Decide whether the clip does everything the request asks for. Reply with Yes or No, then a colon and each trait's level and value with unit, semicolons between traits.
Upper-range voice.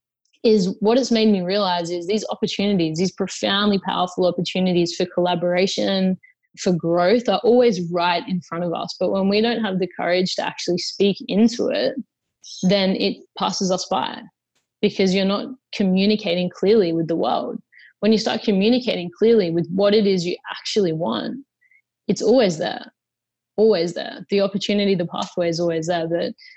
Yes: high, 195 Hz